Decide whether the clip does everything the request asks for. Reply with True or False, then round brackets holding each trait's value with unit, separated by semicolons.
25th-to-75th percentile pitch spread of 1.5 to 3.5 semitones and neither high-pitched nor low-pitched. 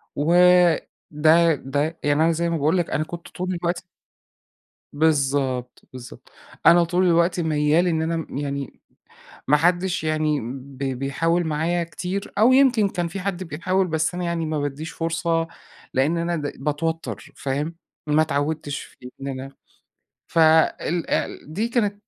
True (3.0 semitones; 160 Hz)